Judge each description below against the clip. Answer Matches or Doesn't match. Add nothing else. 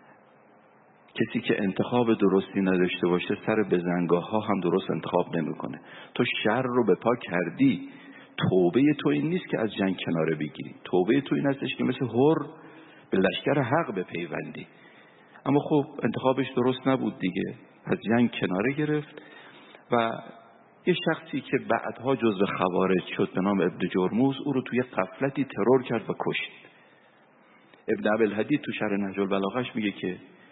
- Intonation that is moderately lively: Doesn't match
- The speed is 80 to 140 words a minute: Doesn't match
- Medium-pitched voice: Doesn't match